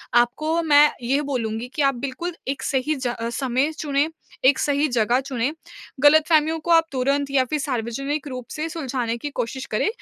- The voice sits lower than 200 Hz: No, very high, 275 Hz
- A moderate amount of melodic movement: Yes, average, 3.2 semitones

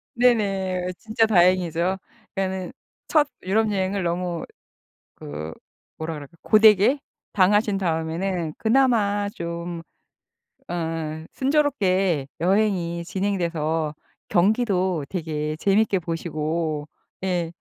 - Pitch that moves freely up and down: No, average, 3.7 semitones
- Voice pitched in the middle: Yes, medium, 180 Hz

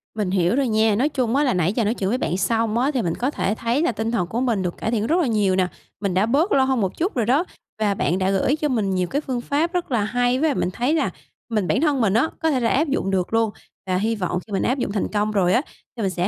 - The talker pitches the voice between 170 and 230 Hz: Yes, high, 225 Hz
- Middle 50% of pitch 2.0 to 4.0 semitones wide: No, average, 5.2 semitones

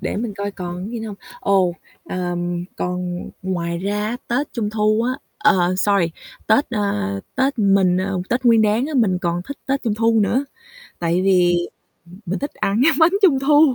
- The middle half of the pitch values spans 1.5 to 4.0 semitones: No, average, 4.8 semitones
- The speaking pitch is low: No, high, 205 Hz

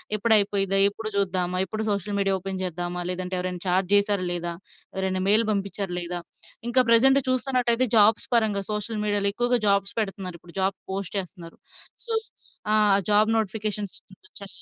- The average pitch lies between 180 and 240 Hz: Yes, high, 200 Hz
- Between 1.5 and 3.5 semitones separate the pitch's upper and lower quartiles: Yes, average, 2.8 semitones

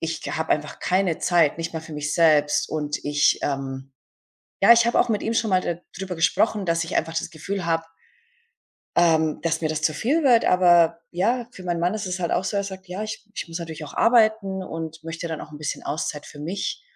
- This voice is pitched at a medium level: Yes, medium, 170 Hz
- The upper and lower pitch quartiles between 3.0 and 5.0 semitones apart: Yes, average, 3.5 semitones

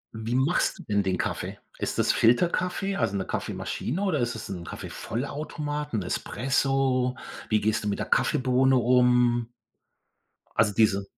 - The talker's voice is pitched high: No, low, 125 Hz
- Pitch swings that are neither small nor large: Yes, average, 3.9 semitones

